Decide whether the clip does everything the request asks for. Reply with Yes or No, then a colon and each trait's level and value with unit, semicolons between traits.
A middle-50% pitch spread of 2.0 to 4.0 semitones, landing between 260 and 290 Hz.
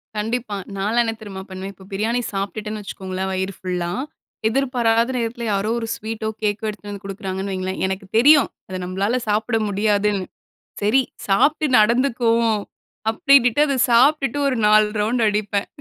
No: average, 3.1 semitones; high, 215 Hz